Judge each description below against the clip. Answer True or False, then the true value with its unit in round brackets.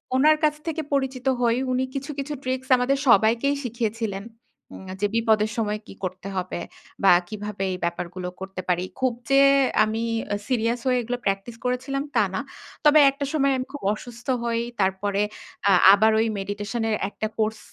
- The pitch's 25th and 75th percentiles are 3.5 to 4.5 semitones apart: True (4.1 semitones)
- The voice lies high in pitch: True (230 Hz)